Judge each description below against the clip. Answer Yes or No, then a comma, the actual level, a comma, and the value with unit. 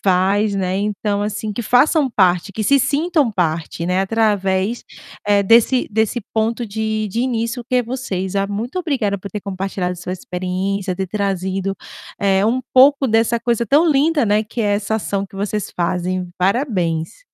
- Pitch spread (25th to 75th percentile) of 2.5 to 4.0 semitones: Yes, average, 3.6 semitones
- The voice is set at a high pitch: Yes, high, 205 Hz